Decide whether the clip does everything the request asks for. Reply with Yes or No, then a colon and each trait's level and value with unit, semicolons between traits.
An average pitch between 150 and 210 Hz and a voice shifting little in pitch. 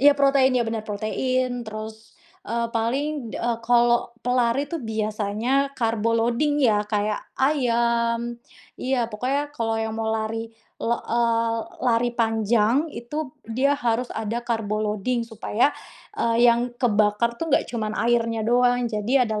No: high, 235 Hz; narrow, 2.0 semitones